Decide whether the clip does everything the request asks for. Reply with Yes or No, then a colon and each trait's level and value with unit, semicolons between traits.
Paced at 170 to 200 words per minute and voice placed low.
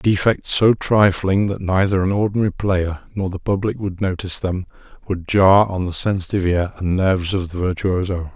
Yes: average, 180 wpm; very low, 95 Hz